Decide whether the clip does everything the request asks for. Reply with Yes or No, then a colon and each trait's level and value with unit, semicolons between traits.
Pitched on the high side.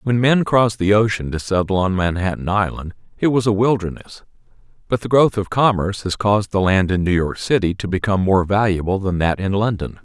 No: low, 100 Hz